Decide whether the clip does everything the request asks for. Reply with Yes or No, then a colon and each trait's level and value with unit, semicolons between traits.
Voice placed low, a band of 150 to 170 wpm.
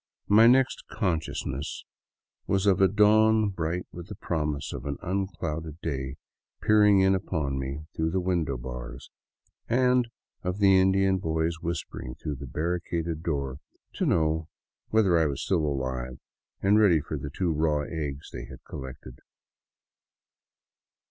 No: very low, 80 Hz; average, 140 wpm